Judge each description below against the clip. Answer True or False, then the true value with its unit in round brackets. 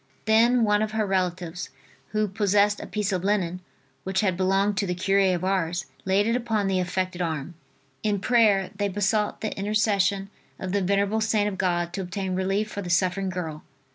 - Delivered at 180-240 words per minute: True (190 wpm)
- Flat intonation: True (2.1 semitones)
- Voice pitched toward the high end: True (195 Hz)